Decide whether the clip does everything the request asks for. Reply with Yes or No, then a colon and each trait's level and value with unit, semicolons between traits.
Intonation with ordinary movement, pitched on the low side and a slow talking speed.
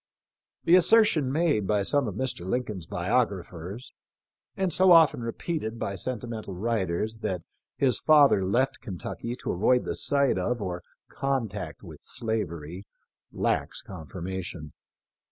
No: wide, 6.0 semitones; low, 110 Hz; slow, 125 wpm